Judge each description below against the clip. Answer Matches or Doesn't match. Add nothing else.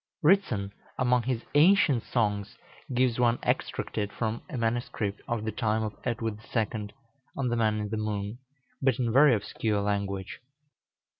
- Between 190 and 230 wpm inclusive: Doesn't match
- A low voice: Matches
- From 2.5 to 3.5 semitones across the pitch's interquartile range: Matches